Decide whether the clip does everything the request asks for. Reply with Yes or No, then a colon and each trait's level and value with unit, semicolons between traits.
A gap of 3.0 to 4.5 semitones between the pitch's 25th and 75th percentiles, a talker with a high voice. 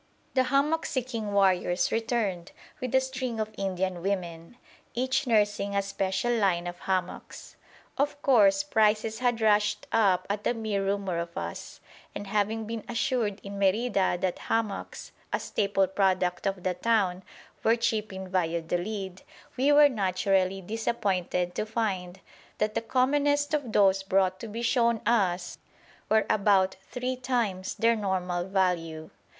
Yes: average, 3.7 semitones; high, 205 Hz